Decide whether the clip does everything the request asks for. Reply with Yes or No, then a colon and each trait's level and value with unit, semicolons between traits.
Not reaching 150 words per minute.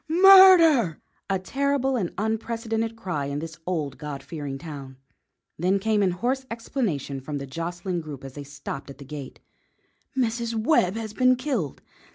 No: average, 160 wpm